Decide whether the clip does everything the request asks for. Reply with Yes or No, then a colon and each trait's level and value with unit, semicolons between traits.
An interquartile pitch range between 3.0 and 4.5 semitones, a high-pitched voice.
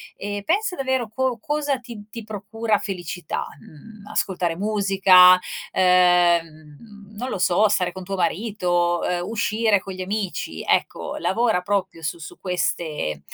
Yes: average, 3.6 semitones; high, 195 Hz